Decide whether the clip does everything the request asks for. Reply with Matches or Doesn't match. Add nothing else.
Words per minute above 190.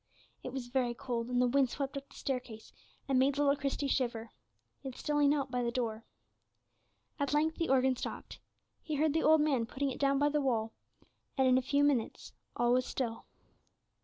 Matches